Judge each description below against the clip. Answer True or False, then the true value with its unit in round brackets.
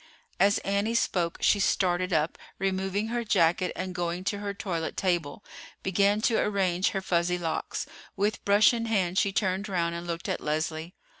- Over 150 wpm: True (170 wpm)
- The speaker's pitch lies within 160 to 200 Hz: True (185 Hz)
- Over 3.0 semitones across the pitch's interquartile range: False (2.7 semitones)